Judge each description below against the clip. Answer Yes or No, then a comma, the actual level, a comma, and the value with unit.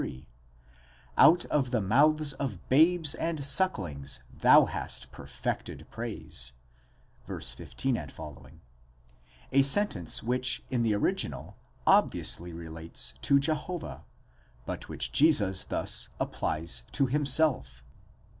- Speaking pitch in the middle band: No, low, 130 Hz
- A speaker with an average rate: No, slow, 105 wpm